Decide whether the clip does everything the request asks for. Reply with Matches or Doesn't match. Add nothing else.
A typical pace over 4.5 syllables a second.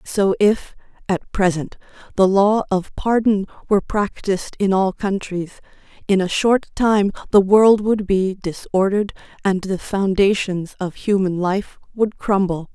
Doesn't match